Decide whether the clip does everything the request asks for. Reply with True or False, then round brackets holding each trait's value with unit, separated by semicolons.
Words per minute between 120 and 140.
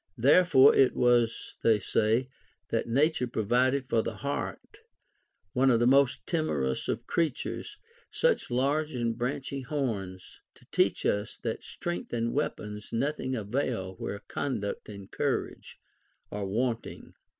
True (135 wpm)